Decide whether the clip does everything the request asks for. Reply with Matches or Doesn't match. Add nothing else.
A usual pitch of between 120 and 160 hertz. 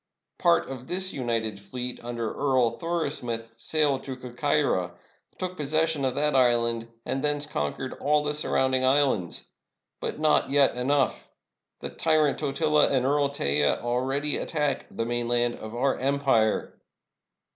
Matches